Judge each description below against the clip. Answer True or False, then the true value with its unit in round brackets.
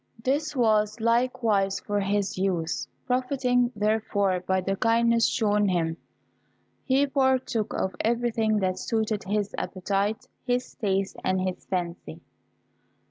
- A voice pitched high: True (210 Hz)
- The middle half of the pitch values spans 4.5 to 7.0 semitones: False (3.7 semitones)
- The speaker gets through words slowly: True (120 wpm)